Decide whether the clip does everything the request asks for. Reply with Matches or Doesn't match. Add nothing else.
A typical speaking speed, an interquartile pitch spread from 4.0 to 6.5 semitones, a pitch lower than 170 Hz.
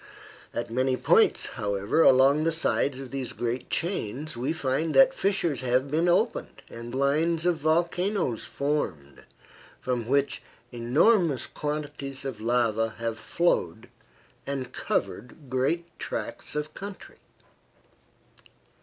Doesn't match